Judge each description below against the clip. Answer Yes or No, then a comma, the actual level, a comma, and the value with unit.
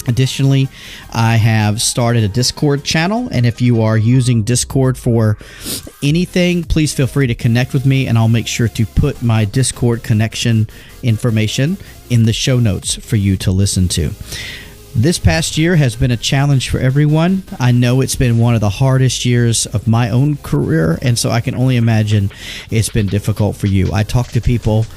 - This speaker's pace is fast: No, average, 185 wpm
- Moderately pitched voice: No, low, 120 Hz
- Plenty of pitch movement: No, average, 3.2 semitones